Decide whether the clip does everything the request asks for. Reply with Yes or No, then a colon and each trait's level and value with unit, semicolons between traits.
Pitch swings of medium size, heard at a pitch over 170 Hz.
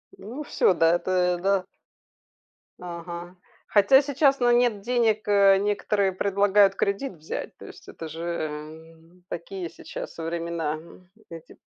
Yes: average, 3.5 semitones; medium, 185 Hz